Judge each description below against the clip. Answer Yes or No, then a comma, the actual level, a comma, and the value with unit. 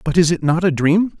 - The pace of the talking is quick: Yes, fast, 300 wpm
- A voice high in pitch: No, medium, 170 Hz